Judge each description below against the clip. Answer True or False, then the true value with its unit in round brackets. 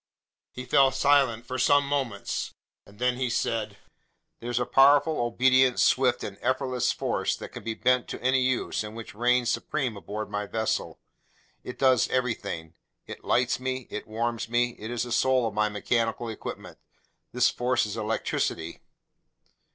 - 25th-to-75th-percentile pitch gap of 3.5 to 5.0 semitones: False (2.5 semitones)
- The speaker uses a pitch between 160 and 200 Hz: False (120 Hz)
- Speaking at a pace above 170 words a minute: False (155 wpm)